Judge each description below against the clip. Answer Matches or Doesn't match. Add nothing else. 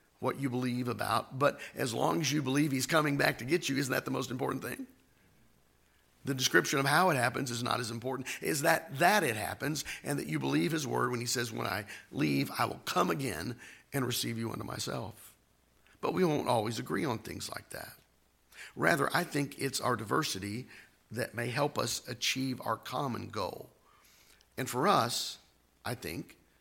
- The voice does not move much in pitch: Doesn't match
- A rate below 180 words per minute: Doesn't match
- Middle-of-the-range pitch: Doesn't match